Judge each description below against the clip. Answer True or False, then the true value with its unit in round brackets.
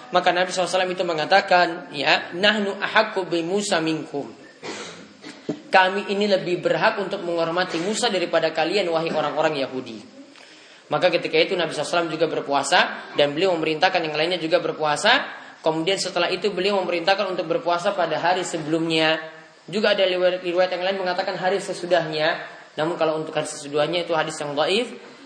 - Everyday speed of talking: False (150 wpm)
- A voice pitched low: False (175 Hz)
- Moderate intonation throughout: True (3.0 semitones)